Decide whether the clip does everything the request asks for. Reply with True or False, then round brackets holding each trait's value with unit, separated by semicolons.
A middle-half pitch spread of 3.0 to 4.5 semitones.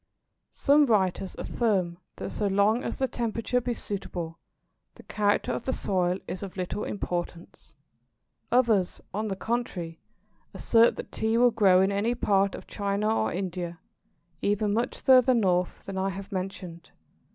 True (3.7 semitones)